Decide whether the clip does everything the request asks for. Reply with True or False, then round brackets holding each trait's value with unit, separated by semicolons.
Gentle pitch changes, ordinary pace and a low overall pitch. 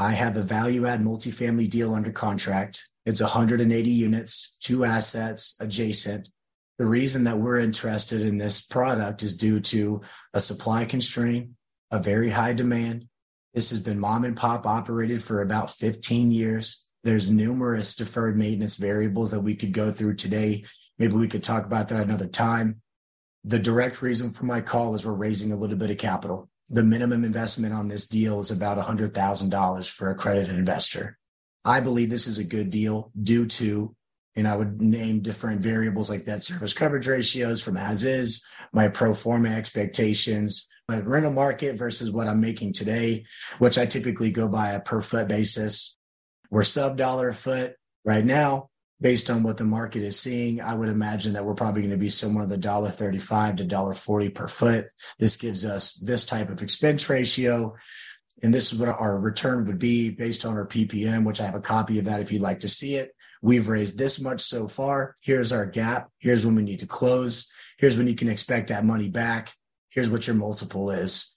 True (2.1 semitones; 190 wpm; 110 Hz)